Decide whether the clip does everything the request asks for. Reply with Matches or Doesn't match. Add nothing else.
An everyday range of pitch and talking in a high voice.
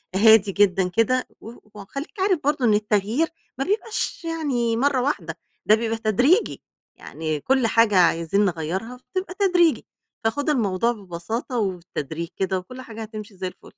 Doesn't match